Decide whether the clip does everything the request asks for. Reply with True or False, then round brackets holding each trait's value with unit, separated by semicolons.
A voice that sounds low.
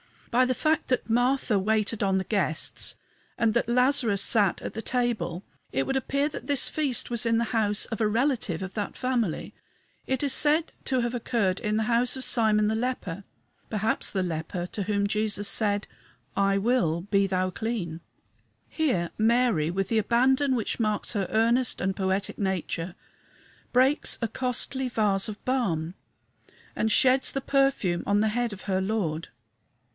False (220 Hz)